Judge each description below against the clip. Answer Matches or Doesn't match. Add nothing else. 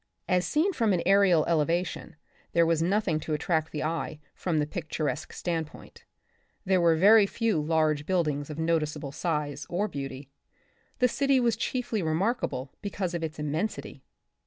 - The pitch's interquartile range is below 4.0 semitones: Doesn't match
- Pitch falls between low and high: Matches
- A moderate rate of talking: Matches